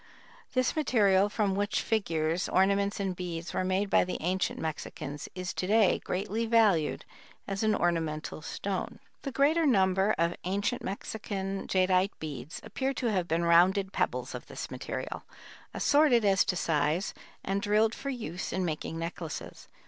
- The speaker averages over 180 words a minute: No, average, 155 wpm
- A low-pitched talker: No, high, 190 Hz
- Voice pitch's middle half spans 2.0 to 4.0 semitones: Yes, average, 3.6 semitones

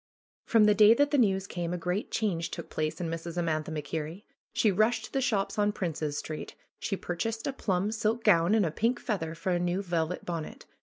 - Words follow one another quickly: Yes, fast, 215 wpm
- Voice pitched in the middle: Yes, medium, 180 Hz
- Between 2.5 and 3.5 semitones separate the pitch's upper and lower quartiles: No, average, 4.4 semitones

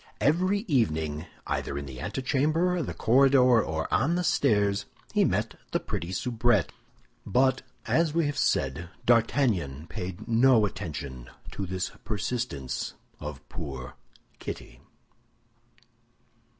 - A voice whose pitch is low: Yes, low, 110 Hz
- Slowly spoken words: Yes, slow, 115 wpm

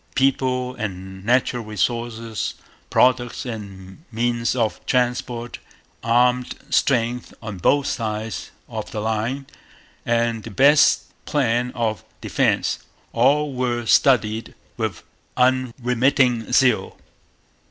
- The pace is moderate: No, slow, 100 wpm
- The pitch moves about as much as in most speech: No, narrow, 2.3 semitones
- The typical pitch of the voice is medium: No, low, 120 Hz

